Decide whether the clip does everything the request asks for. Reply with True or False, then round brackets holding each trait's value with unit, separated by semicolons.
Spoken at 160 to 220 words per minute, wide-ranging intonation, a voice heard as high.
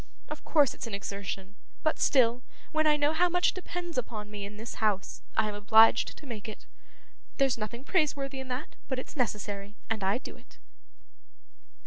True (180 wpm; 5.7 semitones; 235 Hz)